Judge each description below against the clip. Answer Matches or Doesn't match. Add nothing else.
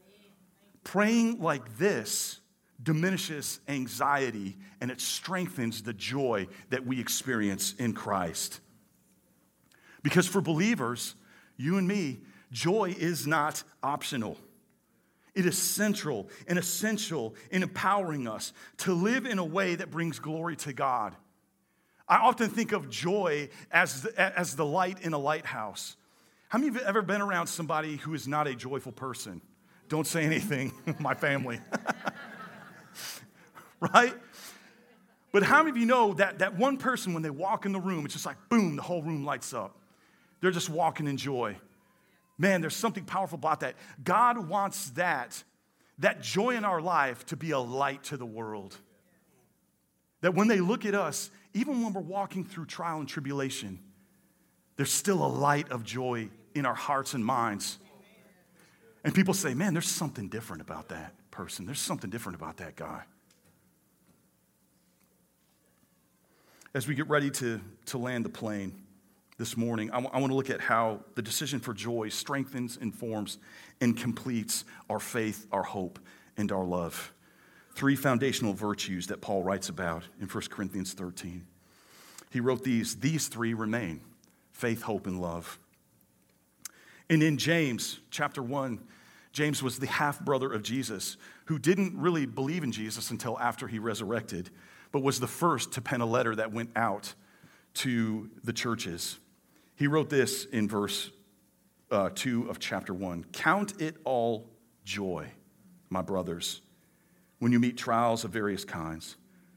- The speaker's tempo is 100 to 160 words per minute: Matches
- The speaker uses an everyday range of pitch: Doesn't match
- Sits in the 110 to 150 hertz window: Matches